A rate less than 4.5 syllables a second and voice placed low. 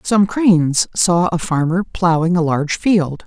No: 4.2 syllables/s; medium, 175 Hz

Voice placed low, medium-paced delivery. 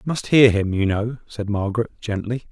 No: low, 110 Hz; fast, 215 wpm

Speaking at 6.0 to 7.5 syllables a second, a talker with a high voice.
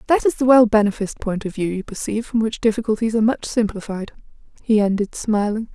Yes: 6.4 syllables/s; high, 220 Hz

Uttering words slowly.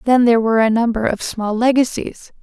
No: average, 200 wpm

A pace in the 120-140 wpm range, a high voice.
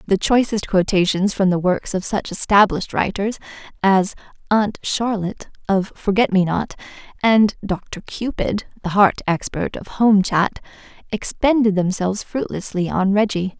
Yes: slow, 135 wpm; high, 200 Hz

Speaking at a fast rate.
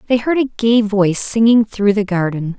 Yes: fast, 210 wpm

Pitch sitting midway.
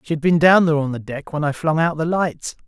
Yes: medium, 155 Hz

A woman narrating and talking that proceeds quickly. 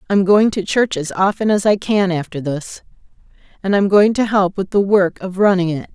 Yes: female; fast, 220 wpm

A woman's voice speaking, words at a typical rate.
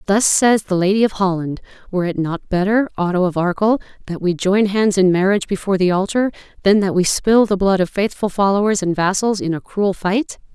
No: female; fast, 210 wpm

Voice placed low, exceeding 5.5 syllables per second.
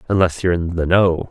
Yes: very low, 85 Hz; 6.2 syllables/s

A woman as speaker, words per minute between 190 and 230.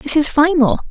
Yes: female; average, 200 wpm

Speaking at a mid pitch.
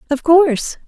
No: very high, 305 Hz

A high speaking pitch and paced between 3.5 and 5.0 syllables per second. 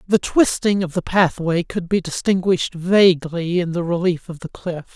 No: medium, 175 Hz; 4.8 syllables/s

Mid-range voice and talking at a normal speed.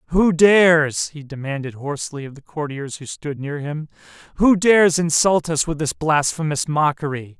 Yes: medium, 155 Hz; average, 155 wpm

